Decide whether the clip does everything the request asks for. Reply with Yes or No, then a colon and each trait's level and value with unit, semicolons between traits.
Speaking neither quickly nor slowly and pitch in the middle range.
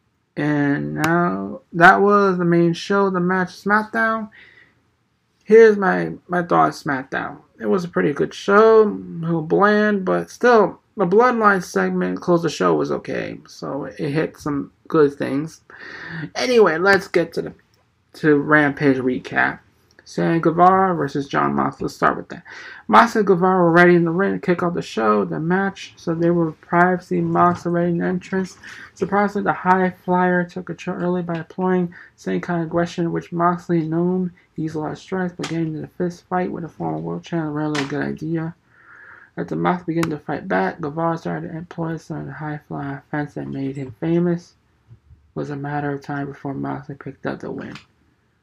Yes: average, 190 wpm; medium, 170 Hz